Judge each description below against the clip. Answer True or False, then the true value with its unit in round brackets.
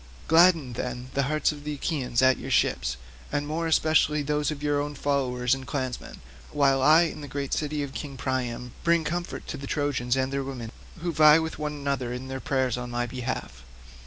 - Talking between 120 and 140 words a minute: False (205 wpm)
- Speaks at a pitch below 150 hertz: True (140 Hz)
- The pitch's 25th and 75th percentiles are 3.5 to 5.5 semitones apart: False (2.7 semitones)